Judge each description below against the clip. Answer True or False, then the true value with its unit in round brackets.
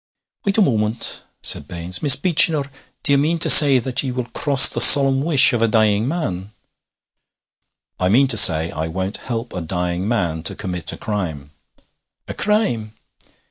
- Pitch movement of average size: False (7.3 semitones)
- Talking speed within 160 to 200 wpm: True (175 wpm)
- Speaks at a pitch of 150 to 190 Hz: False (115 Hz)